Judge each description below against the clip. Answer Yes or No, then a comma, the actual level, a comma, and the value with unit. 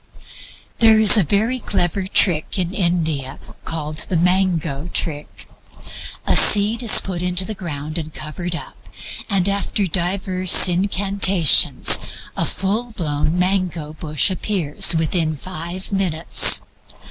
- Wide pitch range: No, average, 3.6 semitones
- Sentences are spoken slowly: Yes, slow, 125 wpm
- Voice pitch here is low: No, medium, 180 Hz